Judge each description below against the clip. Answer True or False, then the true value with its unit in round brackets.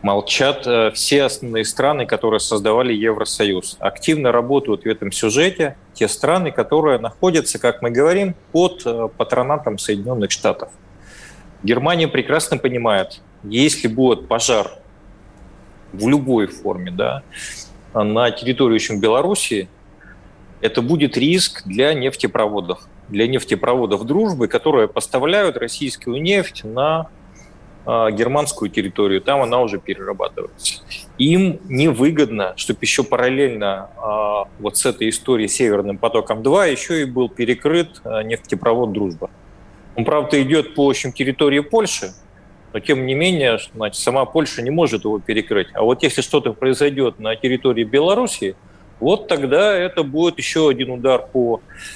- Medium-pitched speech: False (125 Hz)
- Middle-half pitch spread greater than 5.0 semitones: True (5.5 semitones)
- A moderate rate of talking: True (125 wpm)